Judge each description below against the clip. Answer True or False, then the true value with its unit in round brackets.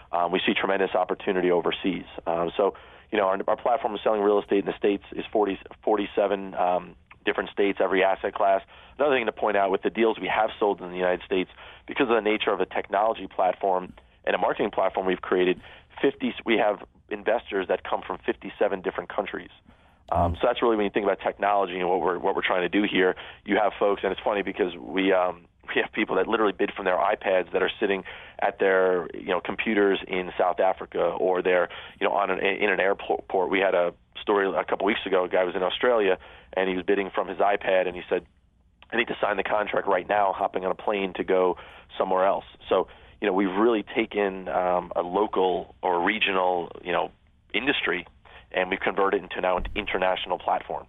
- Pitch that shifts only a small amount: True (1.8 semitones)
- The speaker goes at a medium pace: False (220 wpm)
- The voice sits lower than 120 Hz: True (95 Hz)